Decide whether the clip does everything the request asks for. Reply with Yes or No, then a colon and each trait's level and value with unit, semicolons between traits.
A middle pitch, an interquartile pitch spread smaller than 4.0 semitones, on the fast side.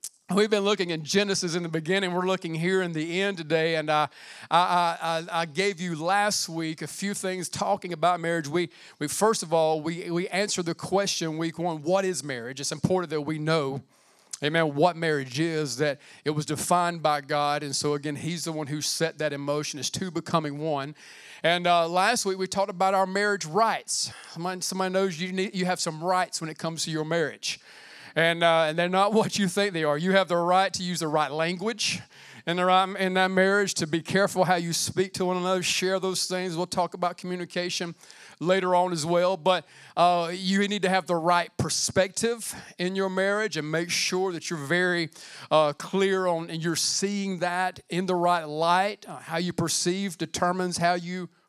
Yes: medium, 175 Hz; narrow, 2.5 semitones; fast, 210 wpm